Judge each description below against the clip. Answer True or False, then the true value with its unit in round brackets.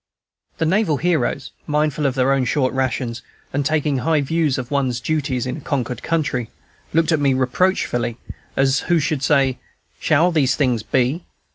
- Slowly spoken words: False (165 wpm)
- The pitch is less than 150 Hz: True (140 Hz)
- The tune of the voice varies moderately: True (3.4 semitones)